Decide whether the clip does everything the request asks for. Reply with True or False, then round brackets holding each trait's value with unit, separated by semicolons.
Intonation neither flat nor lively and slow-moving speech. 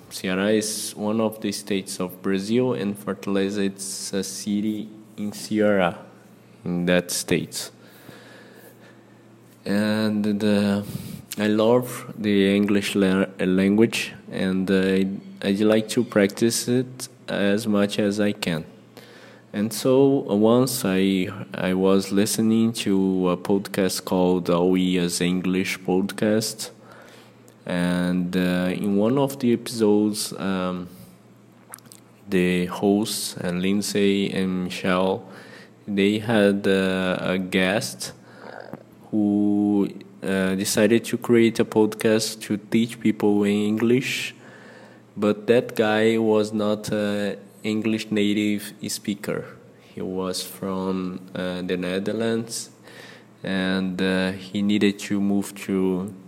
False (2.3 semitones; 115 wpm)